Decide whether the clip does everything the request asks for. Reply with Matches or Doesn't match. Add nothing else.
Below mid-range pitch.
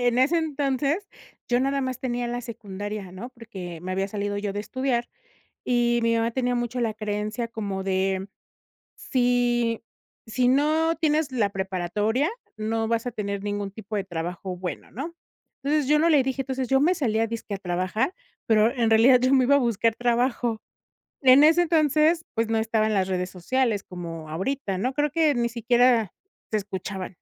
Doesn't match